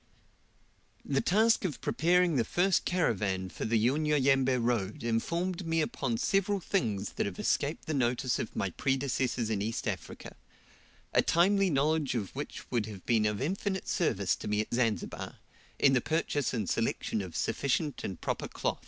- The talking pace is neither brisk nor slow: Yes, average, 165 wpm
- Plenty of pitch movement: Yes, wide, 6.9 semitones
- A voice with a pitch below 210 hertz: Yes, low, 135 Hz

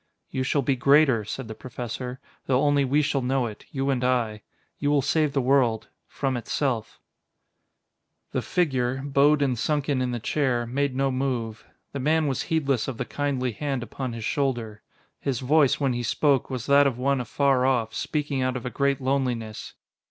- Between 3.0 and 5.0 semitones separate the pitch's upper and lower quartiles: No, narrow, 2.4 semitones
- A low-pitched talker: Yes, low, 130 Hz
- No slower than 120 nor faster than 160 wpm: No, average, 185 wpm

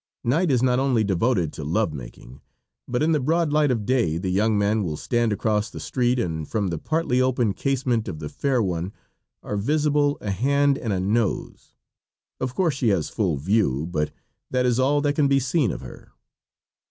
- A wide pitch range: Yes, wide, 6.0 semitones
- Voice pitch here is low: Yes, low, 115 Hz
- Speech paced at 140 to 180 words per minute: No, average, 200 wpm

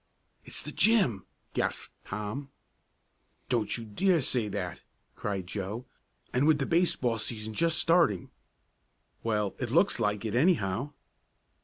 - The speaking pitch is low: Yes, low, 115 Hz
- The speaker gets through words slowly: Yes, slow, 130 wpm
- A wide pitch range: Yes, wide, 6.3 semitones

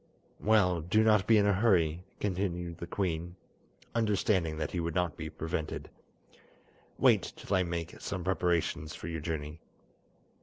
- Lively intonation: No, average, 3.3 semitones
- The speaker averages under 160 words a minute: Yes, average, 150 wpm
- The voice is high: No, very low, 90 Hz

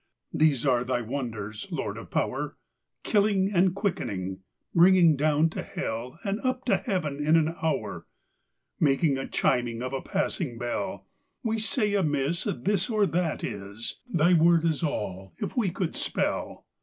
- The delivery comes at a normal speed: No, slow, 130 wpm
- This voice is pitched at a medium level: Yes, medium, 160 Hz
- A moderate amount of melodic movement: No, wide, 7.3 semitones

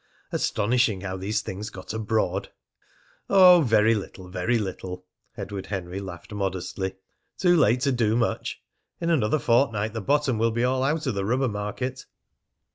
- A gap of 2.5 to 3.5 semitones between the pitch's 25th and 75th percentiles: No, average, 4.6 semitones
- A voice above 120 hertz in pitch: No, low, 110 Hz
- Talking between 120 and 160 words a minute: Yes, average, 155 wpm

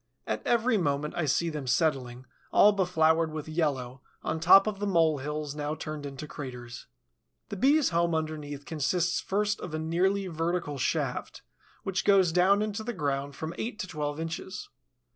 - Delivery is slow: No, average, 170 wpm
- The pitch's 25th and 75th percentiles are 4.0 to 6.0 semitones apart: Yes, average, 4.4 semitones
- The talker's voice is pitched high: No, medium, 160 Hz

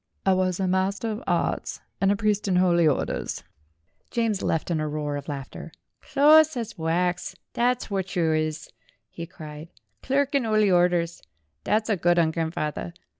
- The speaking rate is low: No, average, 175 wpm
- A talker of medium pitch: Yes, medium, 180 Hz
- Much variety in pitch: No, average, 4.7 semitones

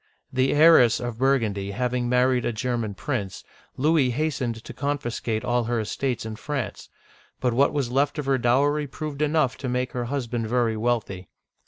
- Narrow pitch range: No, average, 3.0 semitones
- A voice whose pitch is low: Yes, low, 125 Hz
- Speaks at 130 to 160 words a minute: No, average, 170 wpm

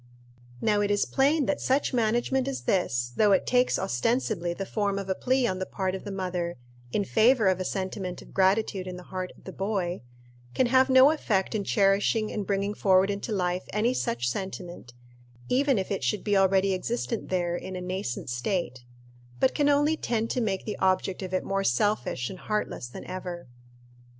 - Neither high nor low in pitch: No, high, 195 Hz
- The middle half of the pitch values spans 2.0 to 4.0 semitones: Yes, average, 3.5 semitones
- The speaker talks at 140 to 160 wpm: No, average, 195 wpm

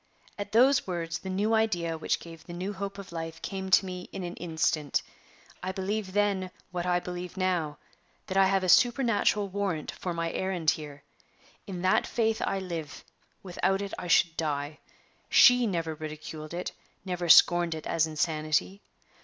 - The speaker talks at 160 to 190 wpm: Yes, average, 170 wpm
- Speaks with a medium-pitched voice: Yes, medium, 180 Hz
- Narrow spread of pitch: No, average, 3.0 semitones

